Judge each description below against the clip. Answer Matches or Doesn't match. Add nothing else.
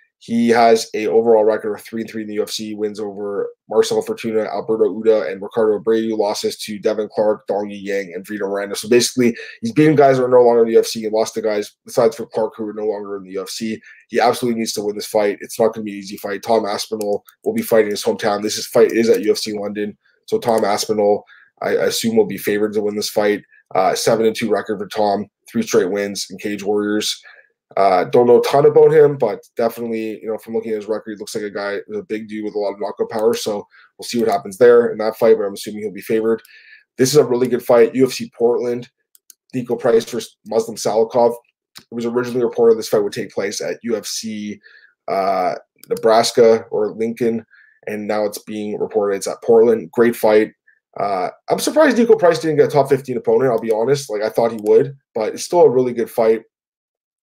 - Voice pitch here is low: Matches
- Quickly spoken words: Matches